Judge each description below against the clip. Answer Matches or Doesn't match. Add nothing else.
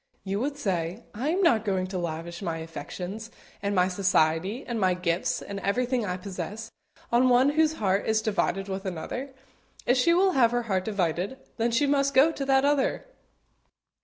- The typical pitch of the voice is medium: Doesn't match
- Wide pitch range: Matches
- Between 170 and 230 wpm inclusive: Matches